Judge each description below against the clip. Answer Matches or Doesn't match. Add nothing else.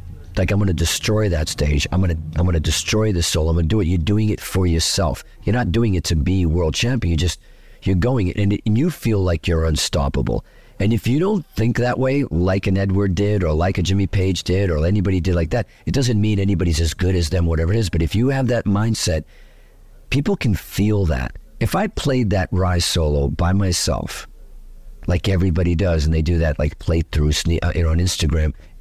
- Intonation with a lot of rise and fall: Doesn't match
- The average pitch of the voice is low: Matches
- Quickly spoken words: Matches